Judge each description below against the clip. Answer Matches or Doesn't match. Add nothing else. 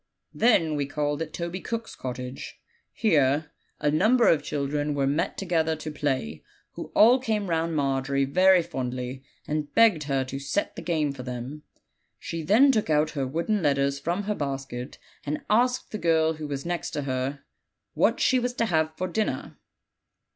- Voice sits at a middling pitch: Matches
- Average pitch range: Matches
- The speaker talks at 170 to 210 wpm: Matches